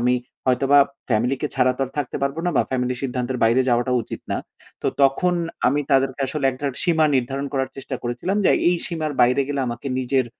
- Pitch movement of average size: No, narrow, 2.1 semitones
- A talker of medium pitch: No, low, 130 Hz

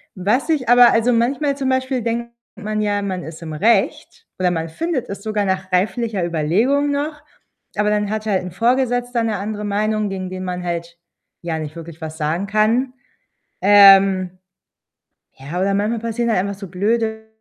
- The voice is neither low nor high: No, high, 210 Hz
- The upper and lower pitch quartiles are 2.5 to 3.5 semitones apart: No, average, 4.2 semitones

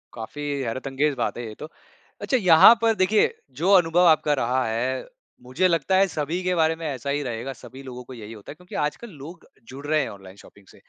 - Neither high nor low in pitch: Yes, medium, 145 Hz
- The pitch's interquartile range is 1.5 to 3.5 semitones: No, wide, 5.5 semitones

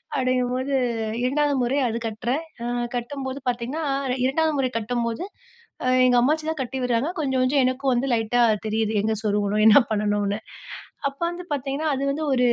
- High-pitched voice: Yes, very high, 255 Hz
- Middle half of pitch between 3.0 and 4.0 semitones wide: Yes, average, 3.3 semitones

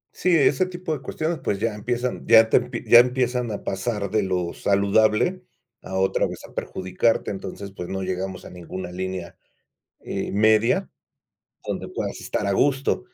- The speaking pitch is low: Yes, low, 105 Hz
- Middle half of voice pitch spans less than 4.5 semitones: No, average, 4.8 semitones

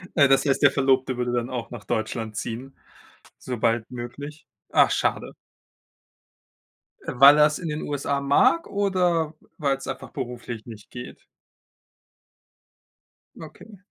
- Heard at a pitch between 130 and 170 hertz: Yes, low, 135 Hz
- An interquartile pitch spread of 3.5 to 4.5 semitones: Yes, average, 3.8 semitones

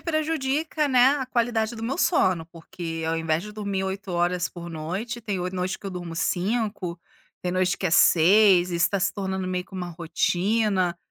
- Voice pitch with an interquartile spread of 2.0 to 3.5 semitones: No, average, 4.1 semitones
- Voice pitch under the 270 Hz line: Yes, high, 190 Hz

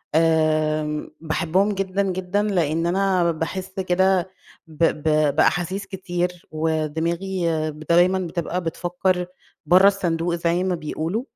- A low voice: No, medium, 175 Hz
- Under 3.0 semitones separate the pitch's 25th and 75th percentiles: Yes, narrow, 2.6 semitones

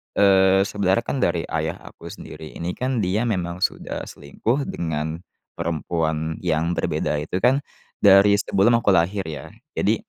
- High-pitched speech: No, very low, 90 Hz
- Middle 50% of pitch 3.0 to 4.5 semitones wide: Yes, average, 3.9 semitones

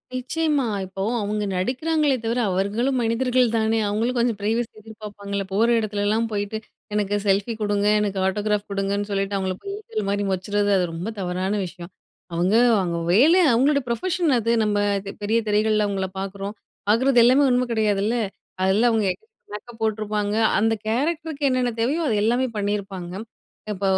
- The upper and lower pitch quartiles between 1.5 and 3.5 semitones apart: Yes, average, 3.2 semitones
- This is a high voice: Yes, high, 210 Hz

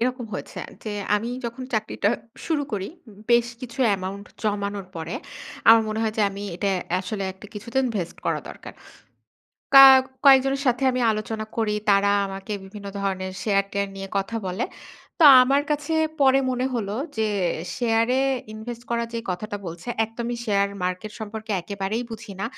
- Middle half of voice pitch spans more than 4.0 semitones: No, average, 3.1 semitones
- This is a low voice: No, high, 215 Hz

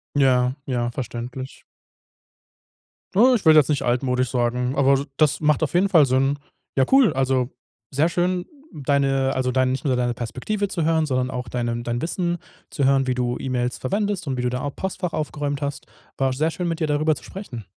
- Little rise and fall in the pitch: No, average, 3.8 semitones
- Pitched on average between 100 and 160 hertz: Yes, low, 135 Hz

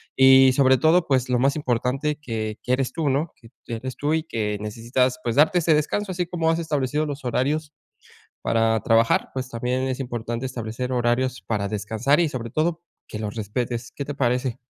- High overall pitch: No, low, 130 Hz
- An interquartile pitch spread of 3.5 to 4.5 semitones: Yes, average, 4.0 semitones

